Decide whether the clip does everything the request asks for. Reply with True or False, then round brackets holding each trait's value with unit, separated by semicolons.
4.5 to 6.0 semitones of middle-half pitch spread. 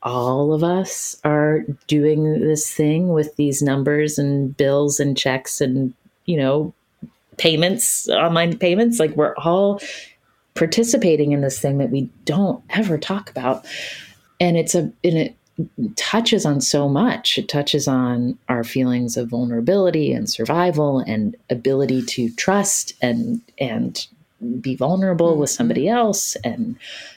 True (5.2 semitones)